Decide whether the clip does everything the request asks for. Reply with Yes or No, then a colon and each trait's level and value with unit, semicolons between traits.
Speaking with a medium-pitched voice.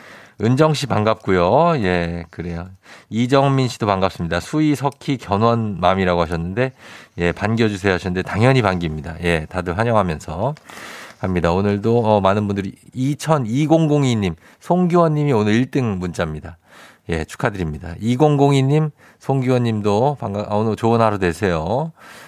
No: low, 105 Hz